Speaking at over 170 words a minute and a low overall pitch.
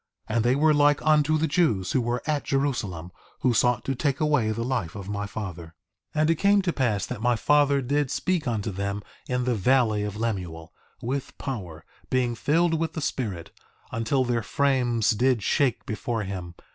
Yes: average, 190 wpm; low, 120 Hz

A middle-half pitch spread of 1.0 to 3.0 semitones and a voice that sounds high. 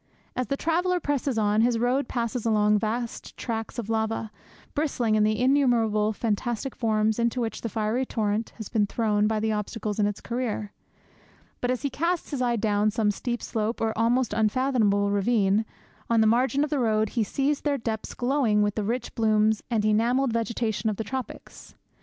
Yes: narrow, 2.6 semitones; high, 225 Hz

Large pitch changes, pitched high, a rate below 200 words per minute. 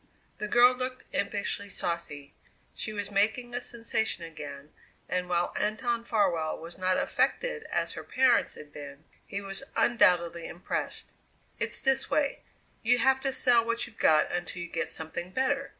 Yes: wide, 6.1 semitones; high, 205 Hz; average, 160 wpm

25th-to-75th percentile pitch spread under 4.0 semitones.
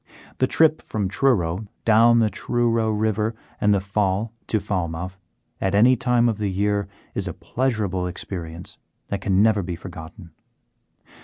Yes: average, 3.3 semitones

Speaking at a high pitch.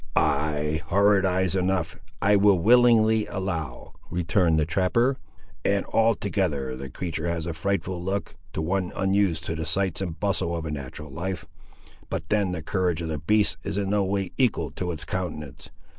No: very low, 90 Hz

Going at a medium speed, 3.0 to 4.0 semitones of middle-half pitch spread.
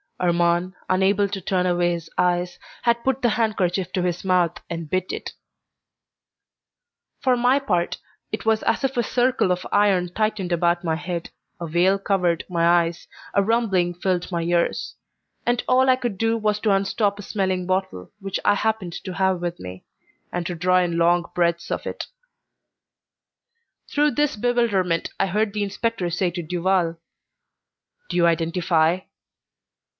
Yes: average, 160 wpm; average, 3.3 semitones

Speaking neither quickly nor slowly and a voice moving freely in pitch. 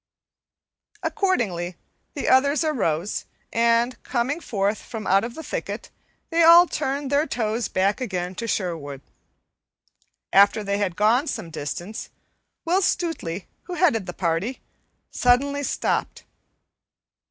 No: slow, 120 wpm; wide, 7.0 semitones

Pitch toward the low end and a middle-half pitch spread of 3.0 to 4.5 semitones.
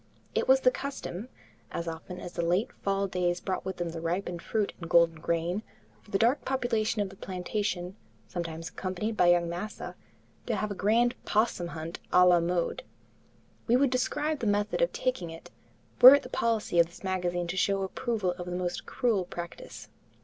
No: medium, 185 Hz; average, 4.1 semitones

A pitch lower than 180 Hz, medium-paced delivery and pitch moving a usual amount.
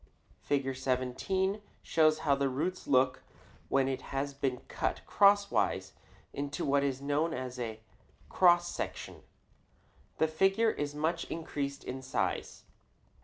No: medium, 140 Hz; slow, 125 wpm; average, 4.0 semitones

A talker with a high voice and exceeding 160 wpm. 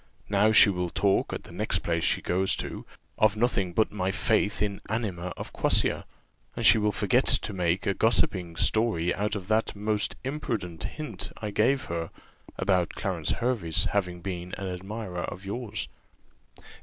No: low, 100 Hz; average, 170 wpm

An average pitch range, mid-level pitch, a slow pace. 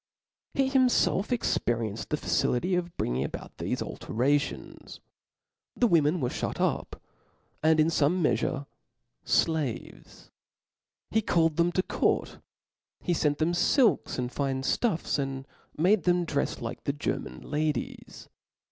Yes: average, 4.5 semitones; medium, 155 Hz; slow, 130 wpm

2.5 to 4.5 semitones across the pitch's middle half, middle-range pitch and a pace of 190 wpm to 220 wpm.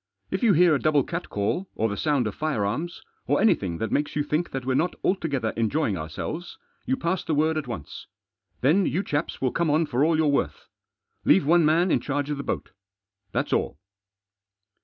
No: average, 5.0 semitones; medium, 150 Hz; average, 200 wpm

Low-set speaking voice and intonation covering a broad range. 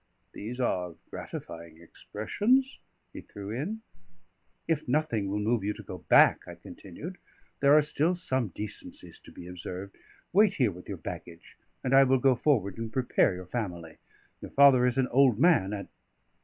Yes: low, 120 Hz; wide, 6.4 semitones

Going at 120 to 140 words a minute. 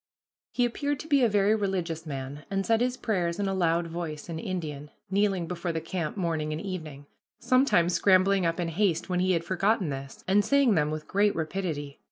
No: fast, 205 wpm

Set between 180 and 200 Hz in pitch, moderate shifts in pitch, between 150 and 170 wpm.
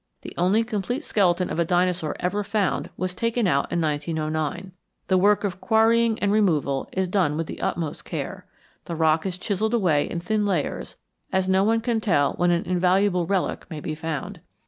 No: medium, 185 Hz; average, 4.0 semitones; average, 190 wpm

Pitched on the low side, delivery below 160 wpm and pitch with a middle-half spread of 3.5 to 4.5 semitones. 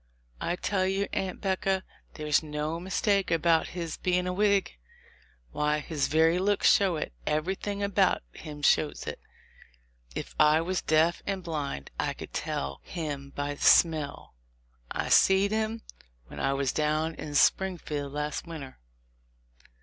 No: medium, 165 Hz; average, 145 wpm; average, 4.1 semitones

